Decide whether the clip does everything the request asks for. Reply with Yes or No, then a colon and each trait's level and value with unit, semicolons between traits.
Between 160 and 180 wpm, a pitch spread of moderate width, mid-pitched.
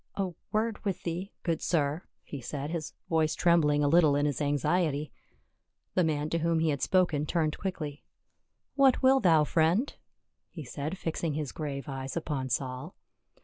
Yes: average, 170 wpm; average, 3.1 semitones; medium, 155 Hz